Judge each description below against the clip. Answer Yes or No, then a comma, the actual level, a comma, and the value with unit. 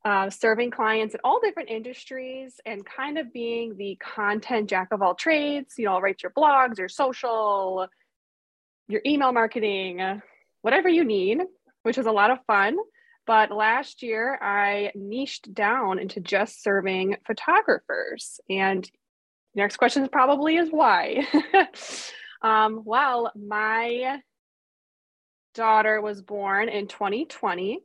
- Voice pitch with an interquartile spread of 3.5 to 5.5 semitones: Yes, average, 4.8 semitones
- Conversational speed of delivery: No, slow, 130 wpm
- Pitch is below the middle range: No, high, 225 Hz